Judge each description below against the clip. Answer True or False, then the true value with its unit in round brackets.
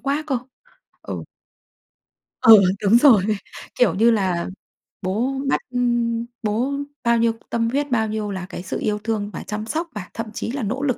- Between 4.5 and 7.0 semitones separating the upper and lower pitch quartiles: False (2.9 semitones)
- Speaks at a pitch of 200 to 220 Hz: False (230 Hz)